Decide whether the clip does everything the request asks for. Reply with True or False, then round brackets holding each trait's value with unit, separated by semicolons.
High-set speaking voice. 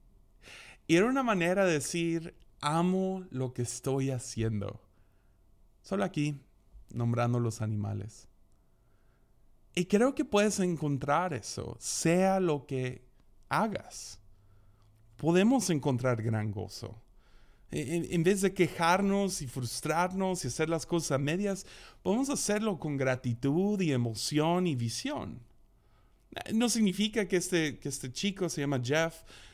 False (140 Hz)